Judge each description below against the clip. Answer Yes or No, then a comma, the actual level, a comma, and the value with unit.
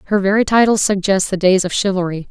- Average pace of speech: No, fast, 210 wpm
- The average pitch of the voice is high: Yes, high, 195 Hz